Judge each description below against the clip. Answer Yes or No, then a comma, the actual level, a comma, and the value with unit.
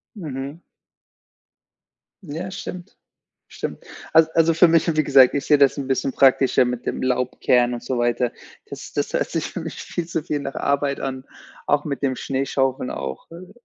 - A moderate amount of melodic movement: Yes, average, 3.7 semitones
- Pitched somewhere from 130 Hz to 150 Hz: Yes, medium, 140 Hz